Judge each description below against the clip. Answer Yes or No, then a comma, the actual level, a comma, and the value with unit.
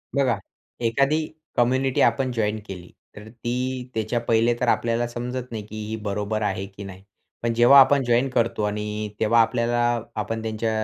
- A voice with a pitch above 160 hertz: No, low, 115 Hz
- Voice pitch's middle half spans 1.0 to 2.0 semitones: No, narrow, 2.4 semitones